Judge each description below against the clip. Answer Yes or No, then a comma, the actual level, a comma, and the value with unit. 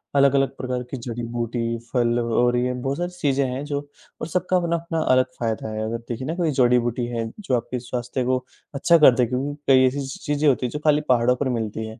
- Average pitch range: Yes, average, 3.0 semitones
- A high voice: No, low, 125 Hz